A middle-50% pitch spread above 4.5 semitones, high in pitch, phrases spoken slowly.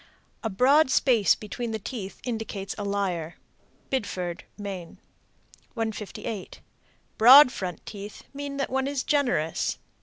Yes: average, 5.0 semitones; high, 220 Hz; slow, 120 wpm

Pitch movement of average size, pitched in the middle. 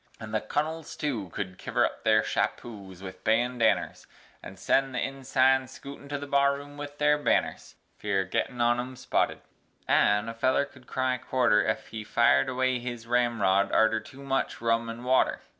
No: average, 3.7 semitones; low, 125 Hz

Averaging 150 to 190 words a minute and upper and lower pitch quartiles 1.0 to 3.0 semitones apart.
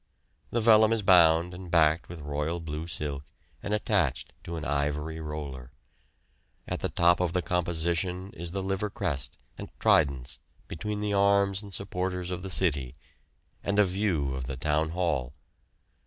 No: average, 160 wpm; average, 4.1 semitones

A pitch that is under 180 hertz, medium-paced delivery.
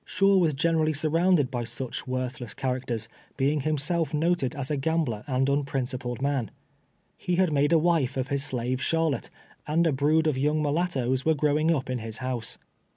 Yes: medium, 140 Hz; average, 175 wpm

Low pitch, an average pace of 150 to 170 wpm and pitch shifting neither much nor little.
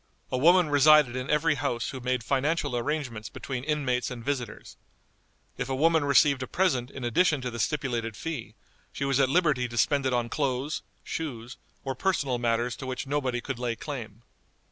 No: low, 130 Hz; average, 185 wpm; average, 3.2 semitones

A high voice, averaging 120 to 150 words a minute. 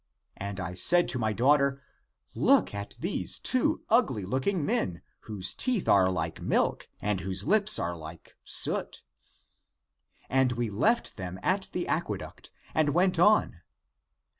No: low, 120 Hz; average, 140 wpm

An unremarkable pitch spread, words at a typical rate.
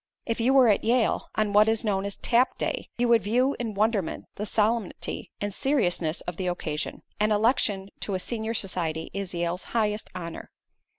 Yes: average, 3.6 semitones; average, 185 wpm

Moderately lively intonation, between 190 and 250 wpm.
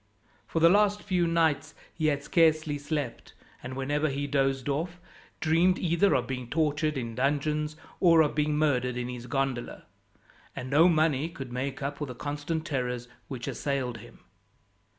No: average, 3.5 semitones; average, 165 wpm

